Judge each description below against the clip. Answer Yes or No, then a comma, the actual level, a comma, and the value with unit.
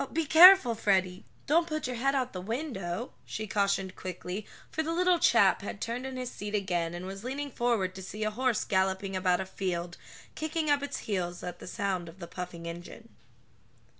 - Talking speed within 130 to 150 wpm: No, average, 200 wpm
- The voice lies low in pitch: No, high, 205 Hz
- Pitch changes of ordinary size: No, wide, 5.9 semitones